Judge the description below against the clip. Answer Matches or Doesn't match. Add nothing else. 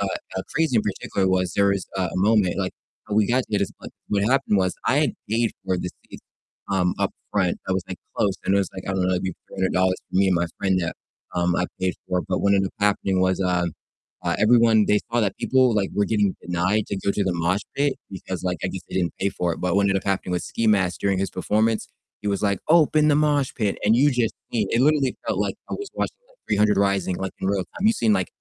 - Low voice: Matches